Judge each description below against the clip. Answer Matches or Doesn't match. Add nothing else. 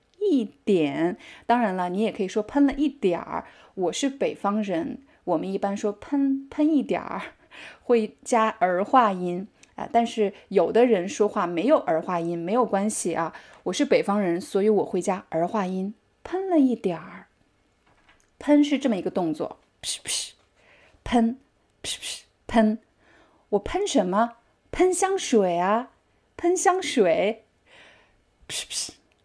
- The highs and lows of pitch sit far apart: Matches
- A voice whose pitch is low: Doesn't match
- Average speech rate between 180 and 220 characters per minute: Matches